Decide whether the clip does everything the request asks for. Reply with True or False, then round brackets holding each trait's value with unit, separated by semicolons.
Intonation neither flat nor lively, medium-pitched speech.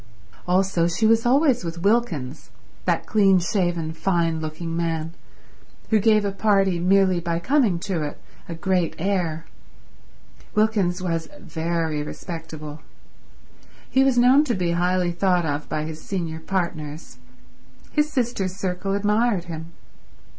True (3.5 semitones; 180 Hz)